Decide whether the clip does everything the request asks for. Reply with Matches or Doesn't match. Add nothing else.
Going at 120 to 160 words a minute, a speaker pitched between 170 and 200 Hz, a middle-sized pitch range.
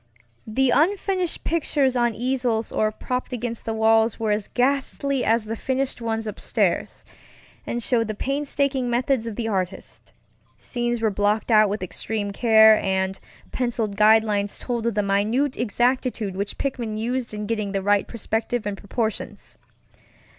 Doesn't match